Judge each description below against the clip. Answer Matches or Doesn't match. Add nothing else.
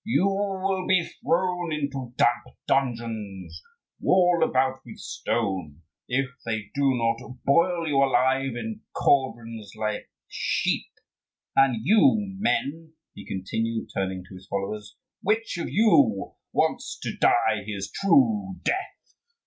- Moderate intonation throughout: Doesn't match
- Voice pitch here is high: Doesn't match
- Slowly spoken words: Matches